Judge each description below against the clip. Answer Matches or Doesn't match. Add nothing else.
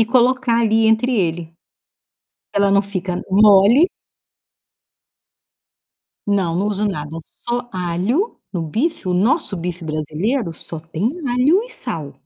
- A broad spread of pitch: Matches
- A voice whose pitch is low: Doesn't match